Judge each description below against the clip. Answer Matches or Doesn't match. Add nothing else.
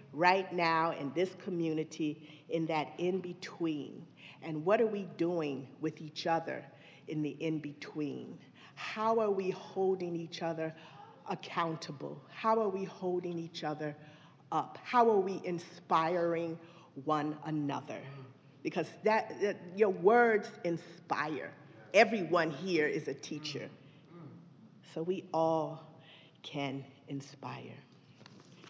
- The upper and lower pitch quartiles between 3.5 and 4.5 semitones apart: Doesn't match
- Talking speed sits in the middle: Doesn't match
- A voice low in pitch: Doesn't match